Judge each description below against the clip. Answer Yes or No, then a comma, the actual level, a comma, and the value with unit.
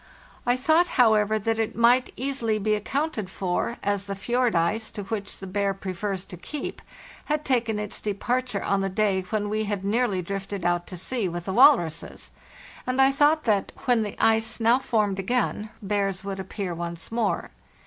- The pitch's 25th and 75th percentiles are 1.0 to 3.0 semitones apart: No, average, 3.7 semitones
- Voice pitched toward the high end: Yes, high, 210 Hz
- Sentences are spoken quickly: No, average, 180 wpm